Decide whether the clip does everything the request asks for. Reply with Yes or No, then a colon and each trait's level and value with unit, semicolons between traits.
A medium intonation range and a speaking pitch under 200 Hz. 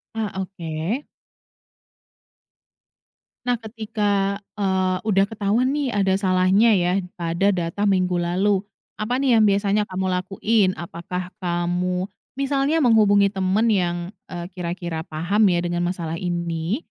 Yes: average, 3.4 semitones; high, 190 Hz